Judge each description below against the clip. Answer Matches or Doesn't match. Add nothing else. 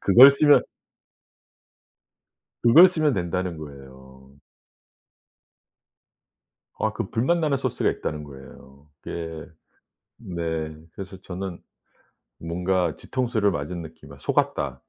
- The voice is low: Matches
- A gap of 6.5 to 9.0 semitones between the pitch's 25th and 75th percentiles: Matches